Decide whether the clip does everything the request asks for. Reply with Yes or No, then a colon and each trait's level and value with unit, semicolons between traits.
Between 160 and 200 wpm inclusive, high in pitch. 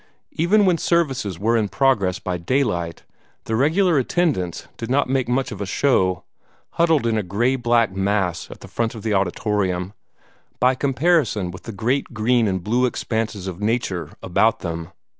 No: average, 170 wpm; low, 115 Hz